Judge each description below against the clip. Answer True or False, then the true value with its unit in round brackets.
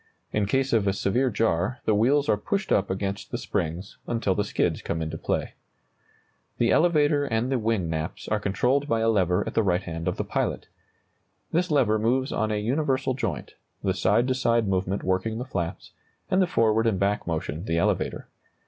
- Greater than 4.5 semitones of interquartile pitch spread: True (5.2 semitones)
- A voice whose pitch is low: True (110 Hz)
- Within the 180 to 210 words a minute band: True (195 wpm)